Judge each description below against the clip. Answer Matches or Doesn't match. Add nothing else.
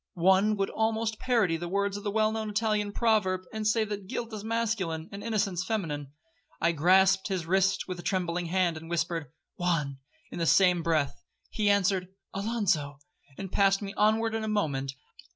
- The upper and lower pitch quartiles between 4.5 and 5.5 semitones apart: Doesn't match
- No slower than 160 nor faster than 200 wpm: Matches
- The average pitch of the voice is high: Matches